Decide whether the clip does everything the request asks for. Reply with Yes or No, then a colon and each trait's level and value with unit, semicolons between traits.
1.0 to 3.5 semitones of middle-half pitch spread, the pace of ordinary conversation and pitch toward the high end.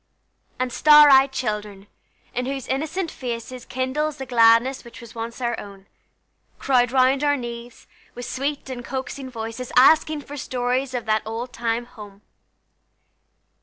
Yes: narrow, 2.6 semitones; average, 145 wpm; very high, 250 Hz